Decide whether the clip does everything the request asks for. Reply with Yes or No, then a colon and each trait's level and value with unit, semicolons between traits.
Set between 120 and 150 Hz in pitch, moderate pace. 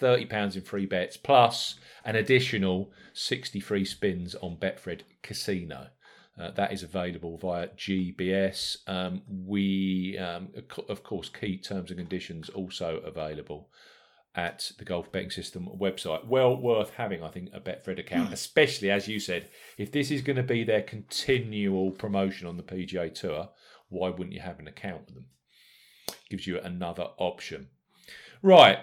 No: very low, 95 Hz; average, 160 wpm